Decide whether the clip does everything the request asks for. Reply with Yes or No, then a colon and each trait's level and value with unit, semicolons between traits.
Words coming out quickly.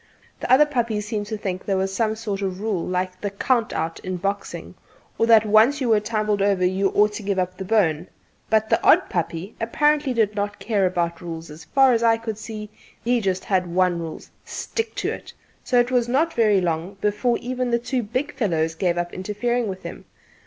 Yes: fast, 215 wpm